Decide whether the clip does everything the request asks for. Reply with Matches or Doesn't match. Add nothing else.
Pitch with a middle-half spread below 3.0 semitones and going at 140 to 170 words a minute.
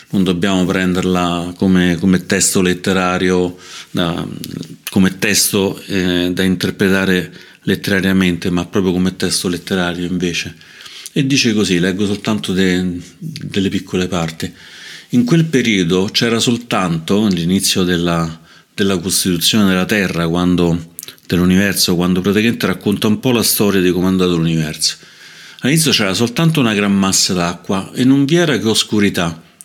Doesn't match